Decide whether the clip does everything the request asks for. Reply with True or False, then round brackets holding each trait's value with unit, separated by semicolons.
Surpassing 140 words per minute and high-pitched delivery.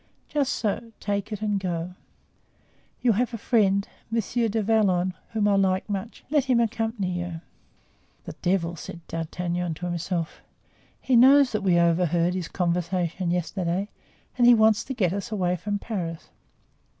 True (155 wpm; 195 Hz)